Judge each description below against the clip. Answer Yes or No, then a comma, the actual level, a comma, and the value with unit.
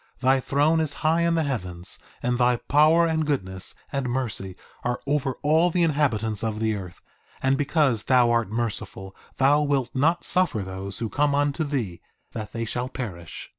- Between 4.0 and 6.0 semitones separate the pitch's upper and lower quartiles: Yes, average, 5.2 semitones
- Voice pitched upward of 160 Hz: No, low, 130 Hz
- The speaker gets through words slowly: No, average, 175 wpm